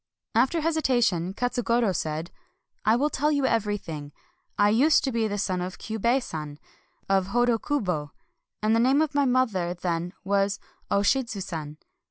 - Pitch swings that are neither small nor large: No, wide, 5.7 semitones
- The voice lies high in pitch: Yes, high, 215 Hz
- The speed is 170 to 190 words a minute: No, average, 160 wpm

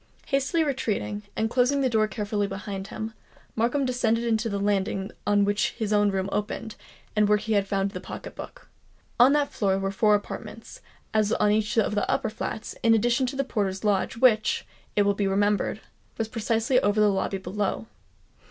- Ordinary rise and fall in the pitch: No, narrow, 2.2 semitones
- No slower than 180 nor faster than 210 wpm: Yes, average, 190 wpm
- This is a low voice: No, high, 210 Hz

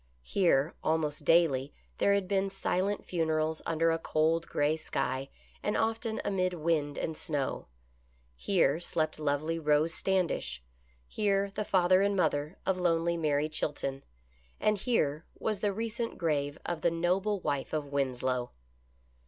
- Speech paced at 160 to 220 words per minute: No, average, 140 wpm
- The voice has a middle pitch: Yes, medium, 165 Hz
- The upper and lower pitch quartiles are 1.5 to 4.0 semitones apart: No, average, 4.6 semitones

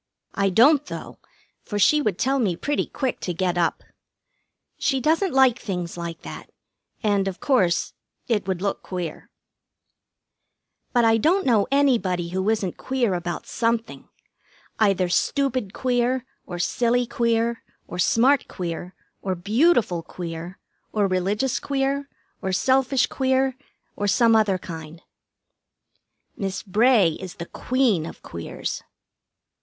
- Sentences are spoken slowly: Yes, slow, 130 wpm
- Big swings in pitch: Yes, wide, 6.1 semitones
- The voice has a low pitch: No, high, 215 Hz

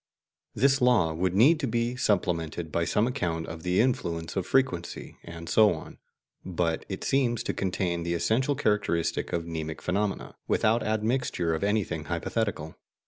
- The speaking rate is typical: Yes, average, 155 wpm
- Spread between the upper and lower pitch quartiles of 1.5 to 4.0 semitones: No, wide, 5.6 semitones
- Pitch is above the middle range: No, very low, 95 Hz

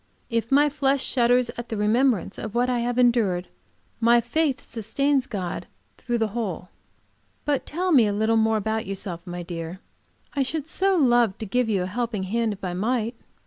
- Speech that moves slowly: No, average, 185 wpm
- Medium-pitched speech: No, high, 230 Hz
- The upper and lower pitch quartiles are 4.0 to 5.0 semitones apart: No, average, 3.6 semitones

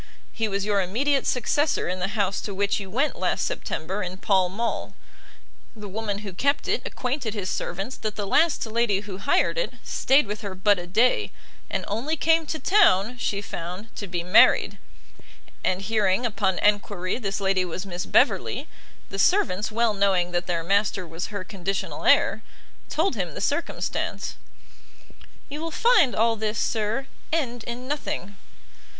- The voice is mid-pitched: No, high, 205 Hz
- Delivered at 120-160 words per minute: No, average, 170 wpm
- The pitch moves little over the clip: No, average, 4.2 semitones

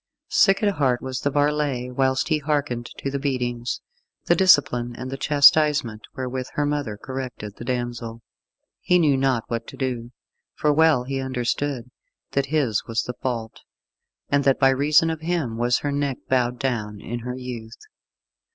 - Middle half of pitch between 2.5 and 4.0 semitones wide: Yes, average, 3.1 semitones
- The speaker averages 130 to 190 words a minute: Yes, average, 170 wpm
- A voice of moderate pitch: No, low, 130 Hz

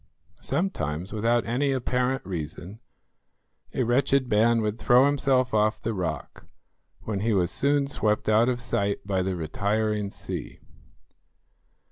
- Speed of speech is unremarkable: No, slow, 130 wpm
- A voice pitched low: Yes, low, 110 Hz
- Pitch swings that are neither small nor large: Yes, average, 4.1 semitones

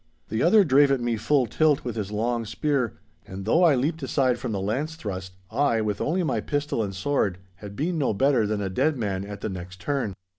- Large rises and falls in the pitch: Yes, wide, 6.0 semitones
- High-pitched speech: No, low, 120 Hz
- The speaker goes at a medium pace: No, fast, 225 wpm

